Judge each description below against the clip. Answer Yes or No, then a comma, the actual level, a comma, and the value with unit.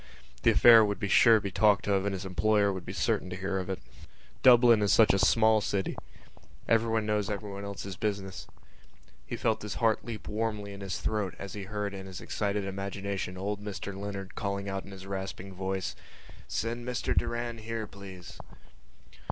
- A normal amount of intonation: No, narrow, 1.9 semitones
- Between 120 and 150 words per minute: No, average, 185 wpm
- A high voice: No, low, 100 Hz